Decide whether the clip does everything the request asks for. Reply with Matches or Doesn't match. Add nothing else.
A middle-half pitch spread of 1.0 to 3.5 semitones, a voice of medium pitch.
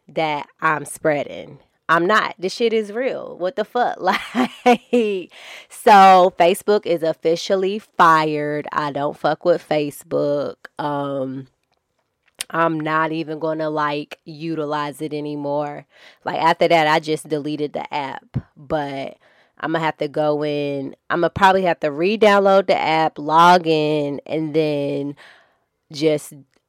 Matches